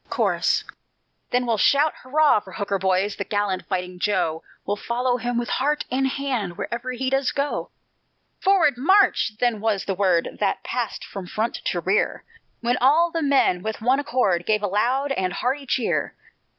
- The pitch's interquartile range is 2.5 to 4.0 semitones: No, average, 5.2 semitones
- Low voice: No, high, 235 Hz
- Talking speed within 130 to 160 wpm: No, average, 175 wpm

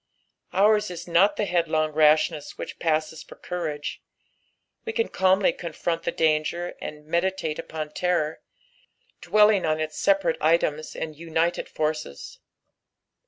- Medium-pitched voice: Yes, medium, 165 Hz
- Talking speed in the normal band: No, slow, 125 wpm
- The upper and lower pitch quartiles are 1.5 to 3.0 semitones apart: Yes, narrow, 2.6 semitones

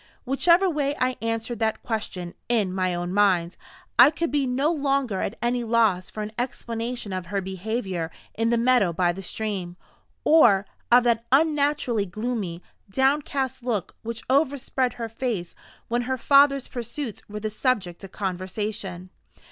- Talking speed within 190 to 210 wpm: No, average, 155 wpm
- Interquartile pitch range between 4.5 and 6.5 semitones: Yes, average, 5.1 semitones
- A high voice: Yes, high, 230 Hz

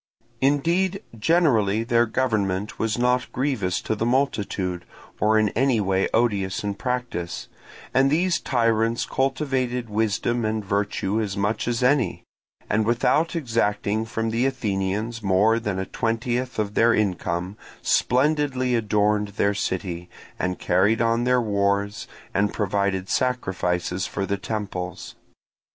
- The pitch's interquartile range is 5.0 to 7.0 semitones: No, average, 3.7 semitones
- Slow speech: Yes, slow, 130 wpm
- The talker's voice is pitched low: Yes, low, 110 Hz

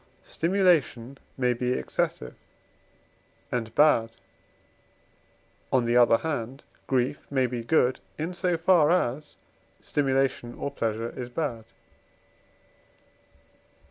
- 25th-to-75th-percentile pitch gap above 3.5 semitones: Yes, average, 4.2 semitones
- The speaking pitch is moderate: No, low, 130 Hz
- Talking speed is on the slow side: Yes, slow, 100 wpm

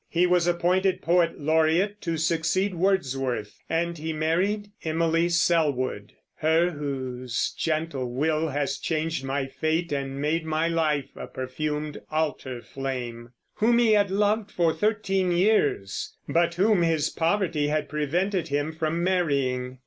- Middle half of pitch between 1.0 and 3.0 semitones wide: No, average, 3.7 semitones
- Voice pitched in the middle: Yes, medium, 160 Hz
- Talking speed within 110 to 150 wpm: Yes, slow, 135 wpm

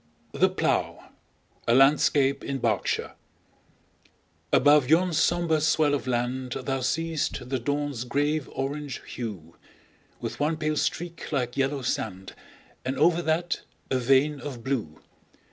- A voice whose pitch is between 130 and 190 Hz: Yes, medium, 140 Hz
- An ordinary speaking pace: No, slow, 130 wpm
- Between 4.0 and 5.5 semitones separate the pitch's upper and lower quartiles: No, average, 3.5 semitones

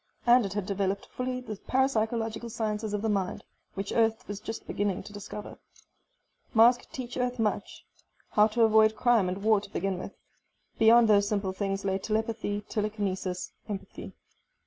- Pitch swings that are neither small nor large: No, narrow, 2.2 semitones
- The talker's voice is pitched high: Yes, high, 215 Hz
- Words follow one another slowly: No, average, 165 wpm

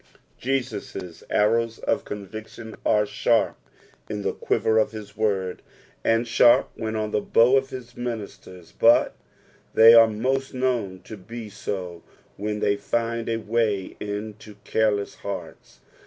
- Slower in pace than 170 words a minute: Yes, average, 140 wpm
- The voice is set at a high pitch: No, low, 110 Hz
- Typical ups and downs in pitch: No, narrow, 2.1 semitones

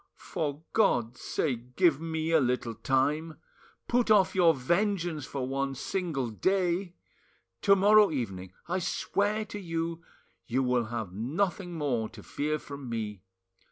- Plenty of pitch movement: Yes, wide, 6.4 semitones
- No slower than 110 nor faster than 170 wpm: Yes, average, 140 wpm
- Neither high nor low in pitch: Yes, medium, 155 Hz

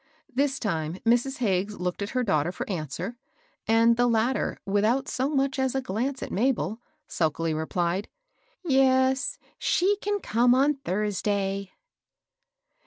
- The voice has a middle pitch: No, high, 230 Hz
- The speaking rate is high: No, average, 145 wpm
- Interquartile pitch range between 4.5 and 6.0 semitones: Yes, wide, 5.5 semitones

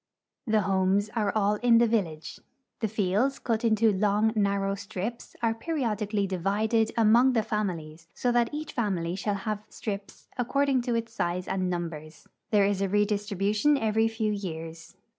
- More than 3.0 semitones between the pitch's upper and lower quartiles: No, average, 2.7 semitones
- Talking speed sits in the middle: Yes, average, 160 wpm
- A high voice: Yes, high, 210 Hz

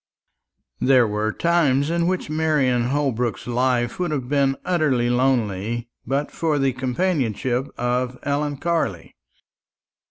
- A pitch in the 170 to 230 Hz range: No, low, 130 Hz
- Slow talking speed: Yes, slow, 120 wpm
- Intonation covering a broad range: No, average, 3.6 semitones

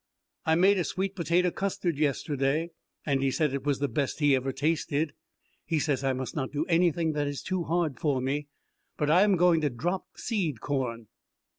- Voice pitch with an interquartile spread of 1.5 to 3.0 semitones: No, average, 3.8 semitones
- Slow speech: No, average, 195 wpm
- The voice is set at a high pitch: No, medium, 150 Hz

